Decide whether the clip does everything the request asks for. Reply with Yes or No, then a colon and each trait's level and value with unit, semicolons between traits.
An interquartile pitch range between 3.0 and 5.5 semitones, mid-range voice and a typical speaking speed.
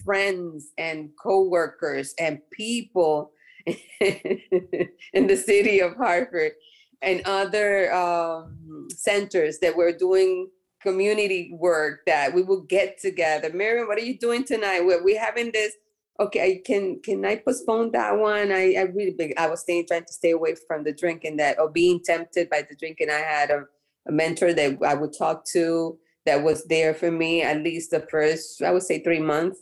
Yes: average, 3.7 semitones; medium, 175 Hz; average, 175 wpm